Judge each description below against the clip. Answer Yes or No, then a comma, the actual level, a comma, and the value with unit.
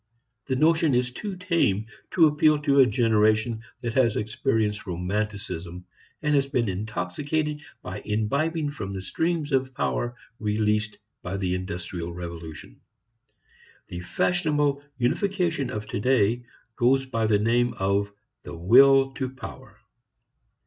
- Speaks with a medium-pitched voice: No, low, 120 Hz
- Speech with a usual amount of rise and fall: No, wide, 5.7 semitones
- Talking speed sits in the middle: No, slow, 130 wpm